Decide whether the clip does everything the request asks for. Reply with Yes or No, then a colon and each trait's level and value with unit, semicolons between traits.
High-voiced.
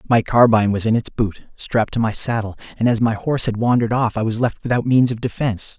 No: low, 115 Hz